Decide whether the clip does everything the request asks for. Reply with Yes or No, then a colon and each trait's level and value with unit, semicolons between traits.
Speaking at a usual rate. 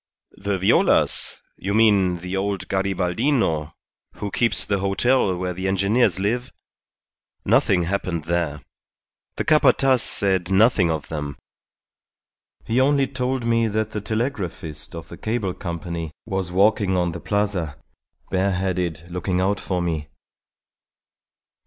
No: slow, 125 wpm